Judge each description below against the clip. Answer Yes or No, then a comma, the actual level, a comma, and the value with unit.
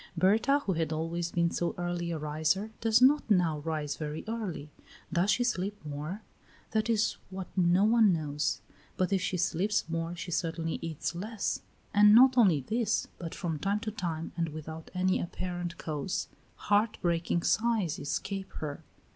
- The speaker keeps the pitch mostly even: No, average, 4.3 semitones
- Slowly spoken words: No, average, 165 wpm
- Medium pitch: Yes, medium, 175 Hz